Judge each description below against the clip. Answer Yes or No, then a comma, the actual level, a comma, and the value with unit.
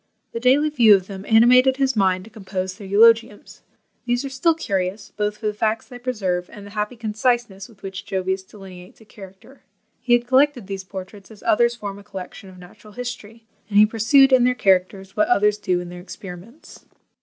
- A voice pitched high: Yes, high, 210 Hz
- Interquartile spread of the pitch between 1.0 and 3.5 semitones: No, average, 4.0 semitones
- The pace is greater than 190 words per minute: Yes, average, 200 wpm